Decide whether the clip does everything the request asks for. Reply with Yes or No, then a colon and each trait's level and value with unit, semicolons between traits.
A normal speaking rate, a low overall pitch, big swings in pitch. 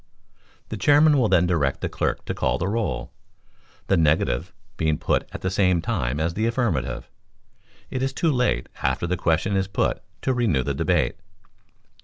Yes: average, 175 wpm; very low, 90 Hz; wide, 6.9 semitones